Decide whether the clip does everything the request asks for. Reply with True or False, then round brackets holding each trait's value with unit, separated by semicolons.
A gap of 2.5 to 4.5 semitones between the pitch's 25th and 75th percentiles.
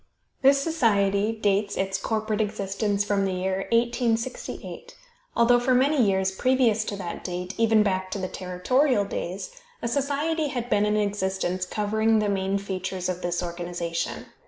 True (3.6 semitones)